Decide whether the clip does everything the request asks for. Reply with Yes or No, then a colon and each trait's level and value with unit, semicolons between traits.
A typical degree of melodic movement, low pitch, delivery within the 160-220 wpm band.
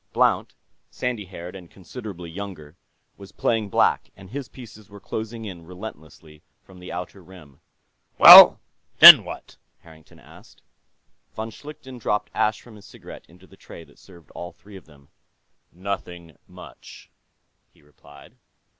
No: average, 4.2 semitones; very low, 95 Hz; average, 145 wpm